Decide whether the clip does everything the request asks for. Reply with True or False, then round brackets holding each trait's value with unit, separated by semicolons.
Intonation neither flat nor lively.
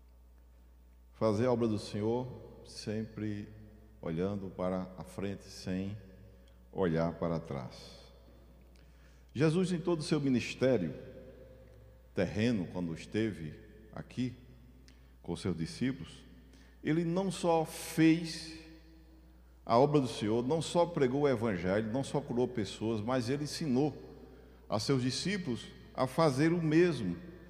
False (8.5 semitones)